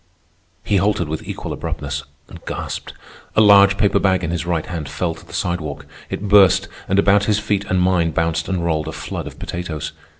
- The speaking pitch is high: No, very low, 90 Hz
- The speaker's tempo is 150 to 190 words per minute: No, average, 200 wpm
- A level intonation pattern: No, average, 3.3 semitones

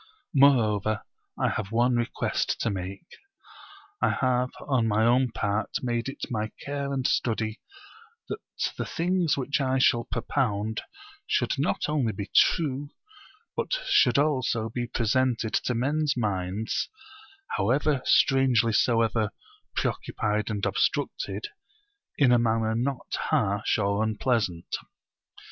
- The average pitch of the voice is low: Yes, low, 120 Hz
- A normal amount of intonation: Yes, average, 3.6 semitones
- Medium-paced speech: No, slow, 120 wpm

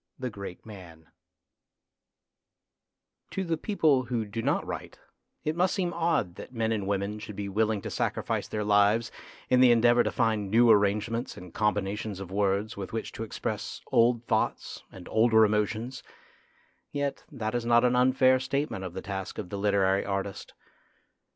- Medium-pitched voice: No, low, 110 Hz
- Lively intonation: No, average, 3.4 semitones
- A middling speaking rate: Yes, average, 165 wpm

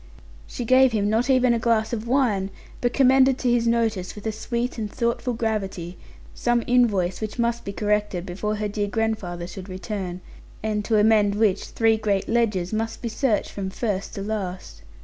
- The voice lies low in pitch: No, high, 220 Hz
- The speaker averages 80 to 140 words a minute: No, average, 185 wpm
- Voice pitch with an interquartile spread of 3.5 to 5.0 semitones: No, average, 2.8 semitones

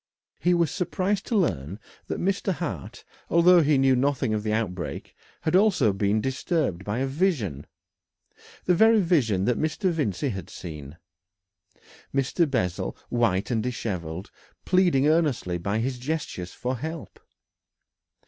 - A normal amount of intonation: No, wide, 8.9 semitones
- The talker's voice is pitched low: Yes, low, 130 Hz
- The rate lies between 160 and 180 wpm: No, average, 140 wpm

